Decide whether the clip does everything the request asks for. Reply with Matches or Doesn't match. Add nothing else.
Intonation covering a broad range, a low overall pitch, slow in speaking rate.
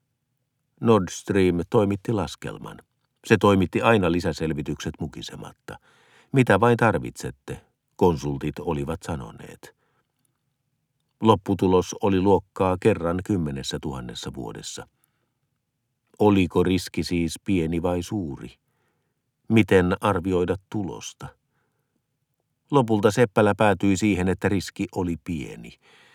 Matches